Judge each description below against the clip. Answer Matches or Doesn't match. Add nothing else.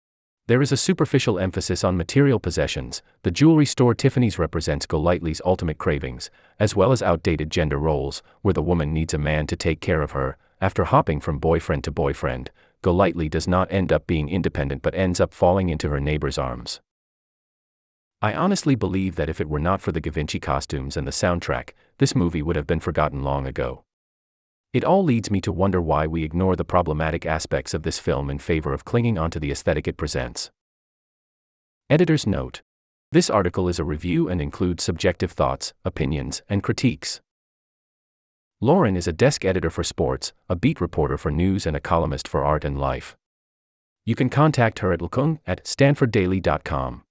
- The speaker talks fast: Doesn't match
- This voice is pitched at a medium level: Doesn't match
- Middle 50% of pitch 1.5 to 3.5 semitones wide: Doesn't match